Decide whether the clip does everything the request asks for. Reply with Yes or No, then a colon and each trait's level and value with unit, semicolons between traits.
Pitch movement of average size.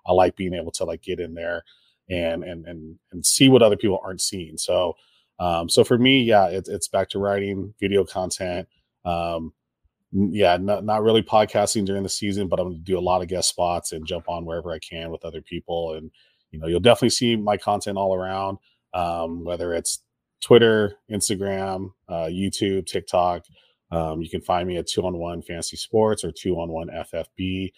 Yes: average, 3.0 semitones